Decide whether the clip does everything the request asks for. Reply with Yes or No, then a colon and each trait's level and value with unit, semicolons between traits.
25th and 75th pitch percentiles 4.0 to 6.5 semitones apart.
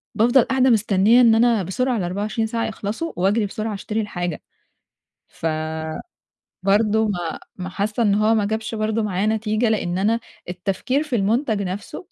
No: average, 2.9 semitones